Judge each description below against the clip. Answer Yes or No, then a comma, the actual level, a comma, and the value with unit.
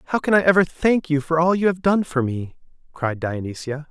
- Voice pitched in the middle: Yes, medium, 160 Hz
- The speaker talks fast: Yes, fast, 230 wpm